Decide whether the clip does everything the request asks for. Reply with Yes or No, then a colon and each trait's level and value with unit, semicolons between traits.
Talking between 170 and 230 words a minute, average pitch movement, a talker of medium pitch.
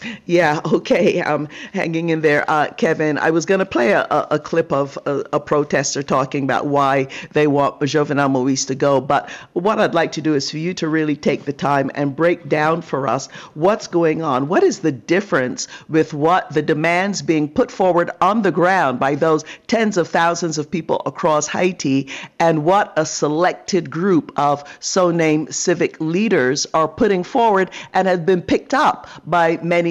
Yes: average, 190 wpm; average, 3.4 semitones; medium, 160 Hz